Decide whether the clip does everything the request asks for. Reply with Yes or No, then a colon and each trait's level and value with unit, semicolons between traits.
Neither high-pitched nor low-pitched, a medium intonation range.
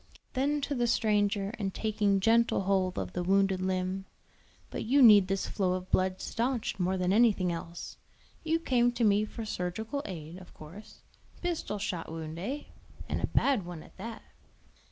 No: high, 200 Hz; average, 4.0 semitones